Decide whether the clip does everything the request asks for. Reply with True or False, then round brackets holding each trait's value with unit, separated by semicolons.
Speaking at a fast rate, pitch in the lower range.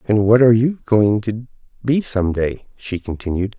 False (185 wpm; 110 Hz)